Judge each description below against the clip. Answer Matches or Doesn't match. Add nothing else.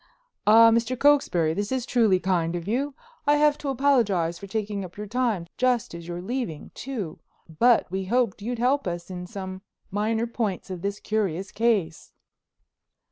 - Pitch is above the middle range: Matches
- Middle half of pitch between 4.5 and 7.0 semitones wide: Matches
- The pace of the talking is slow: Doesn't match